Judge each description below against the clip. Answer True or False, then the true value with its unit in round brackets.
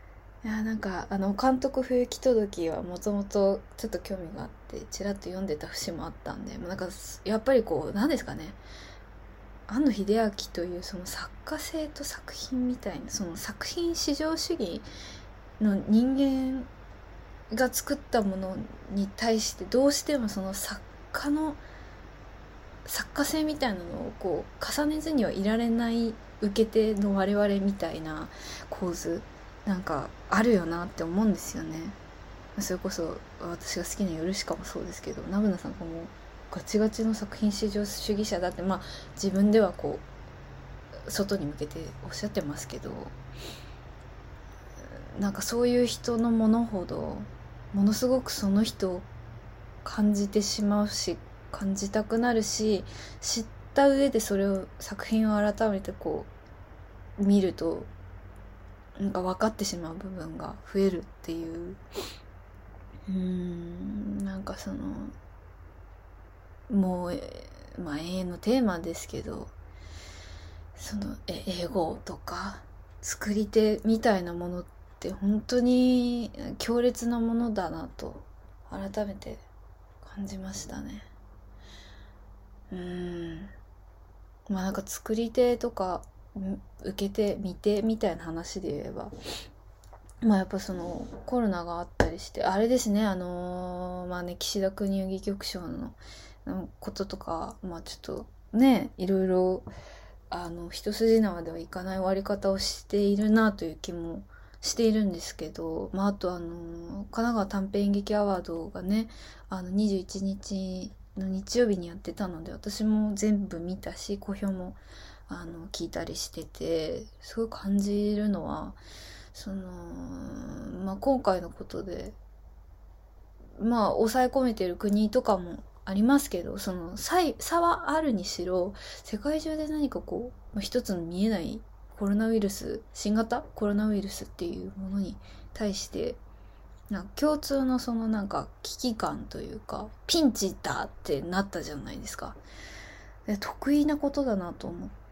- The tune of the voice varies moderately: True (5.0 semitones)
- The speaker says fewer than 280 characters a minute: True (265 characters per minute)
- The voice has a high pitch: True (195 Hz)